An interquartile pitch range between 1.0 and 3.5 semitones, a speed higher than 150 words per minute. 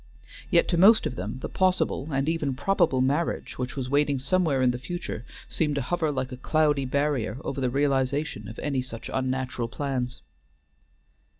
Yes: average, 2.8 semitones; average, 175 wpm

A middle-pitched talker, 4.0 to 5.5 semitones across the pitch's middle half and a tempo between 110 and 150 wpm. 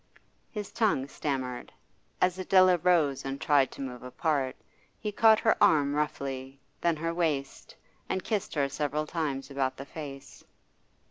Yes: medium, 150 Hz; average, 4.5 semitones; average, 145 wpm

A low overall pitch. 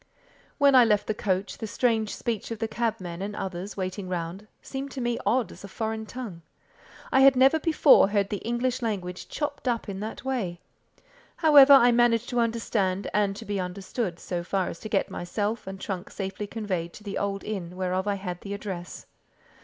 No: high, 210 Hz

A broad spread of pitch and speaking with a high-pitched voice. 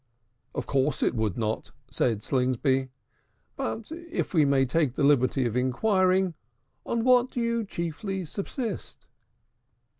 No: wide, 8.7 semitones; medium, 150 Hz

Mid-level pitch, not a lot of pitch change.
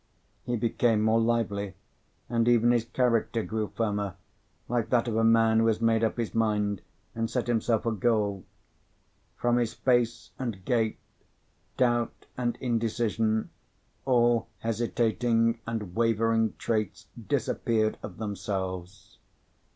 No: low, 115 Hz; narrow, 1.5 semitones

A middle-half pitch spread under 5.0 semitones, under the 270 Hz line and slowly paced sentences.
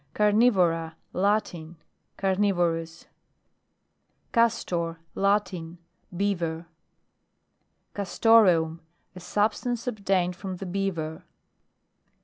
Yes: average, 3.6 semitones; medium, 185 Hz; slow, 65 wpm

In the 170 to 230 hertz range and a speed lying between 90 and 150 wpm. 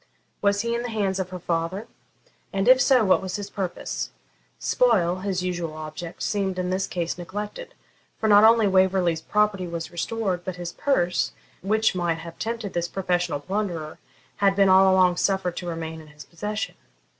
No: medium, 185 Hz; average, 180 wpm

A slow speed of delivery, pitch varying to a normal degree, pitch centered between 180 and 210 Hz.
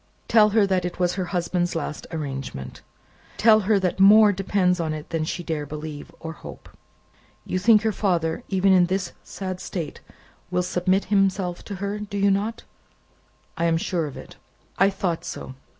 No: average, 180 wpm; average, 3.2 semitones; medium, 185 Hz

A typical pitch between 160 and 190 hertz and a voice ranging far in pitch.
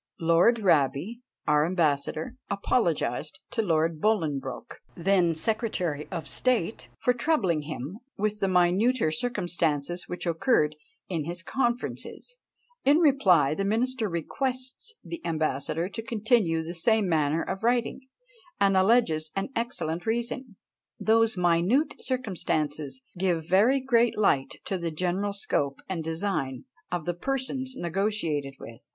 Yes: medium, 185 Hz; wide, 6.3 semitones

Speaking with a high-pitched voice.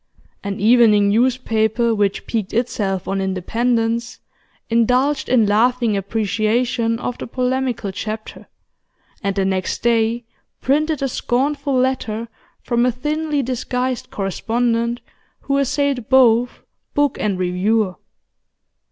Yes: high, 235 Hz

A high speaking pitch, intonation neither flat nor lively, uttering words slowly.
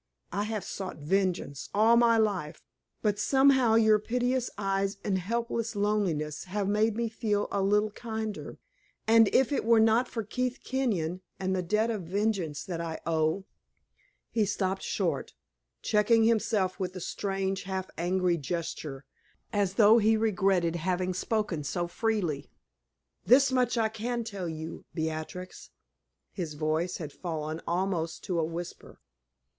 No: high, 195 Hz; average, 4.2 semitones; average, 150 wpm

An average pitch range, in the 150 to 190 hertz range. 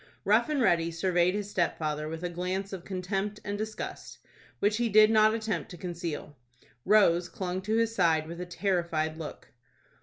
Yes: average, 3.7 semitones; medium, 185 Hz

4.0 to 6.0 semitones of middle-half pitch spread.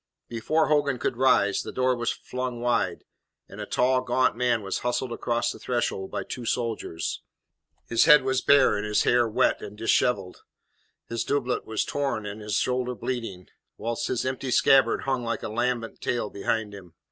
No: narrow, 2.5 semitones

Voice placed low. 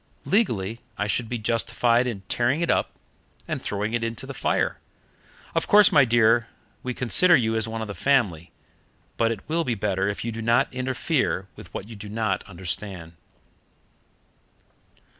Yes: low, 115 Hz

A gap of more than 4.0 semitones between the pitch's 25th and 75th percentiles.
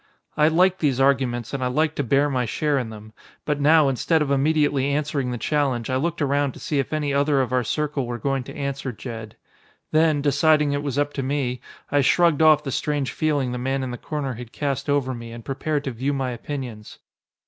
No: average, 2.7 semitones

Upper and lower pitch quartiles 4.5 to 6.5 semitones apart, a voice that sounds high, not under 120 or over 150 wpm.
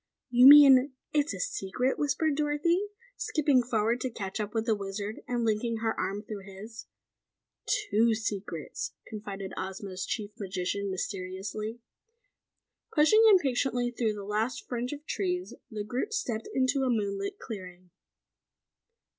Yes: average, 4.9 semitones; high, 225 Hz; slow, 135 wpm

